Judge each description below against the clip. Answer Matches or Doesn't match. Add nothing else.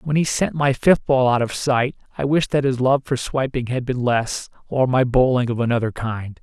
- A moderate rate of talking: Doesn't match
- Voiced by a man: Matches